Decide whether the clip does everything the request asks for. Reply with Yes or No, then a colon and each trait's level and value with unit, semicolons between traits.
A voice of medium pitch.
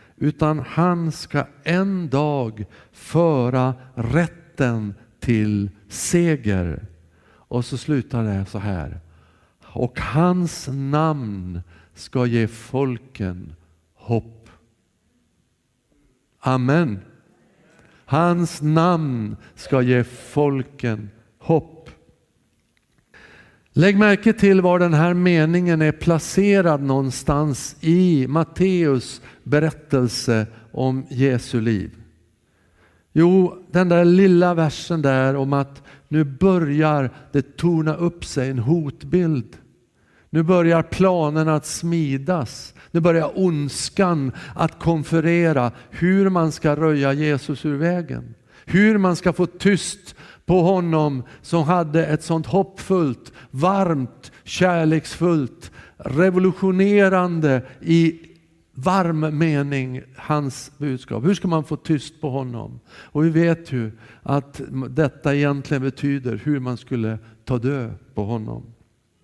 Yes: medium, 145 Hz